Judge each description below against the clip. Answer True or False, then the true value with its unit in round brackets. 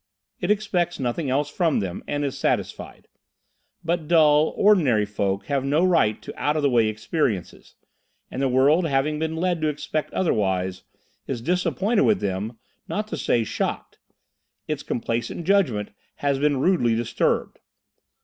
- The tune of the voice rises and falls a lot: True (6.4 semitones)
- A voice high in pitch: False (145 Hz)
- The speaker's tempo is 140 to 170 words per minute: True (150 wpm)